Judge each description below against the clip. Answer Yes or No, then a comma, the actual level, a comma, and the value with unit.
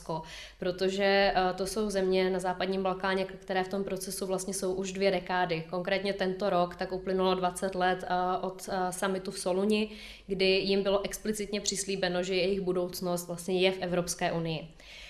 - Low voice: No, high, 190 Hz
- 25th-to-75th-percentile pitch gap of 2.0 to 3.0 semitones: No, narrow, 1.2 semitones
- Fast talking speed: No, average, 160 wpm